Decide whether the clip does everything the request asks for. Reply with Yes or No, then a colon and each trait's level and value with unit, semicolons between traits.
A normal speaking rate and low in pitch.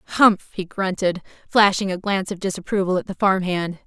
No: average, 185 wpm; high, 190 Hz